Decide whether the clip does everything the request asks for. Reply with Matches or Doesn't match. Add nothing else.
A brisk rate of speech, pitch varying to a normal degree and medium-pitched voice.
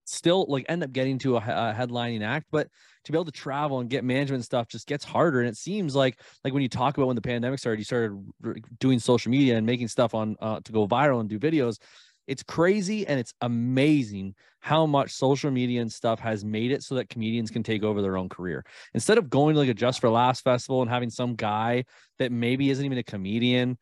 Doesn't match